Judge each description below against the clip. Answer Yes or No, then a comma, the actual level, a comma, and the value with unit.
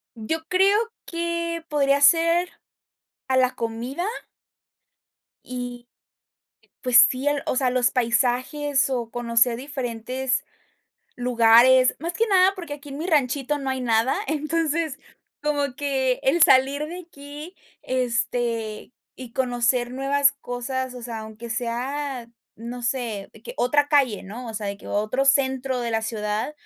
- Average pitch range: Yes, average, 3.3 semitones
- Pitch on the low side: No, very high, 260 Hz